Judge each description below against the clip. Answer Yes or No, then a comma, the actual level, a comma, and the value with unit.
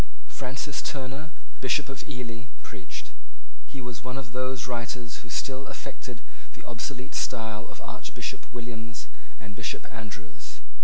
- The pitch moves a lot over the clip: No, narrow, 2.4 semitones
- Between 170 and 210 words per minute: No, slow, 135 wpm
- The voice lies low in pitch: Yes, low, 120 Hz